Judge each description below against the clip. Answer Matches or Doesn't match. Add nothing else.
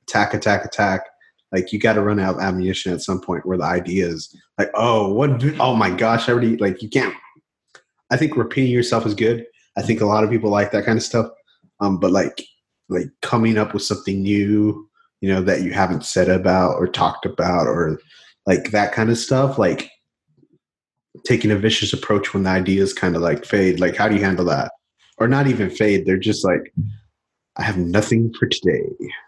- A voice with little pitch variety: Doesn't match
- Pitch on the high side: Doesn't match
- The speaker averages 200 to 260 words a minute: Matches